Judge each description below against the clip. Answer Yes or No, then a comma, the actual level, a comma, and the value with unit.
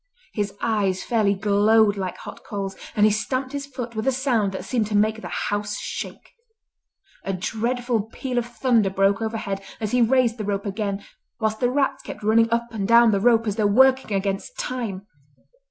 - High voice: Yes, high, 220 Hz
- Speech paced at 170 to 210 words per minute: Yes, average, 190 wpm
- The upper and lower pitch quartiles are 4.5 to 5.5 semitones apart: No, average, 3.1 semitones